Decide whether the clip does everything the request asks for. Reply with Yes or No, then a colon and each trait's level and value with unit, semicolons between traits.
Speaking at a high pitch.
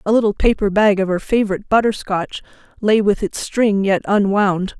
Yes: high, 200 Hz